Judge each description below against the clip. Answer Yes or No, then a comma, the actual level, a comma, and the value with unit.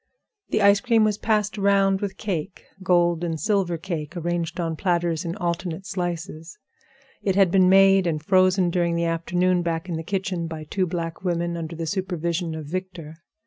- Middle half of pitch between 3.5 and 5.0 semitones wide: No, narrow, 2.5 semitones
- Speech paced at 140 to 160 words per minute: No, average, 175 wpm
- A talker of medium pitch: Yes, medium, 175 Hz